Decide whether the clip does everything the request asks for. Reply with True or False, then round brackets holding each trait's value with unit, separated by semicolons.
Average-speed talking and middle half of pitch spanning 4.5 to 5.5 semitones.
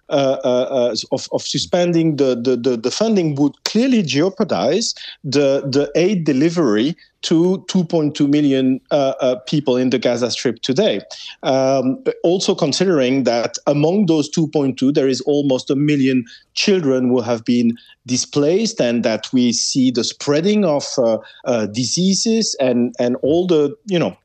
True (155 wpm; 5.1 semitones)